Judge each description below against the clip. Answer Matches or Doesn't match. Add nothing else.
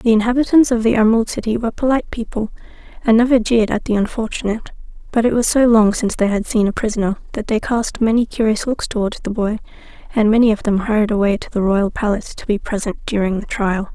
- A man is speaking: Doesn't match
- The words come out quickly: Matches